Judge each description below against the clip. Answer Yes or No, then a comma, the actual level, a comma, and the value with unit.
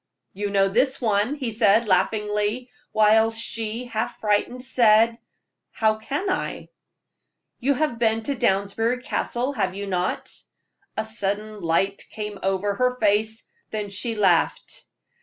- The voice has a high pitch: Yes, high, 220 Hz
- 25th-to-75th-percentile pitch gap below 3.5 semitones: Yes, average, 2.7 semitones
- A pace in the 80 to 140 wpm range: Yes, slow, 135 wpm